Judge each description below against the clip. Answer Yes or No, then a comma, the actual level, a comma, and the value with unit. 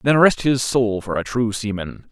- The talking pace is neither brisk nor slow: No, fast, 225 wpm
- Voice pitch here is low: Yes, low, 115 Hz